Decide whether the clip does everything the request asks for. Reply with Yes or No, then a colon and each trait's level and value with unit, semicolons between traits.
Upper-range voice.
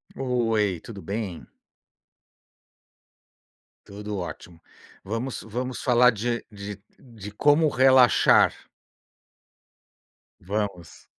No: low, 110 Hz